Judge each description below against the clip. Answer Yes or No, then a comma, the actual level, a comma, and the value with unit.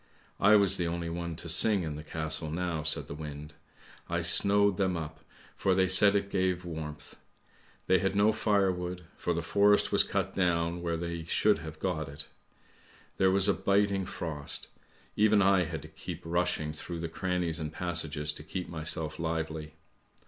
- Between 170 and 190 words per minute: Yes, average, 180 wpm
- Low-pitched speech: Yes, very low, 85 Hz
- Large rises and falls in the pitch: No, average, 3.1 semitones